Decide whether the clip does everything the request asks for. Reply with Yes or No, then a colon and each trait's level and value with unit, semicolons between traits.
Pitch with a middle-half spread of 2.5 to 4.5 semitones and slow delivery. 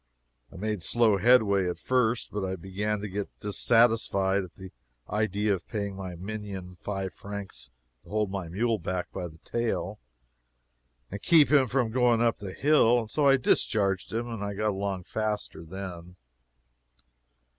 No: average, 3.0 semitones; average, 160 wpm